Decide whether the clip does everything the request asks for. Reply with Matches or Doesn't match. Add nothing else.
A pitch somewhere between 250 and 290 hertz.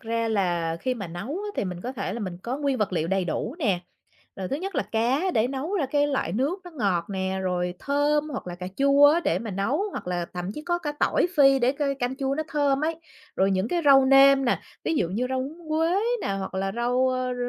Matches